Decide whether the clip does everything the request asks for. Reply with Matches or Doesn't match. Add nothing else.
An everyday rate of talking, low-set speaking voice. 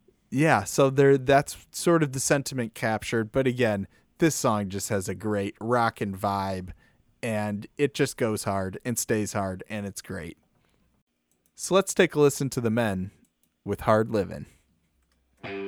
Matches